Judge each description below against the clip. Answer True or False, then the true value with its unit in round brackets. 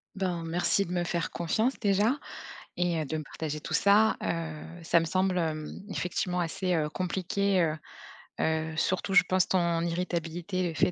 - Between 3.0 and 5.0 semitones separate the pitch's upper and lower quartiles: False (2.4 semitones)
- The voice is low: False (175 Hz)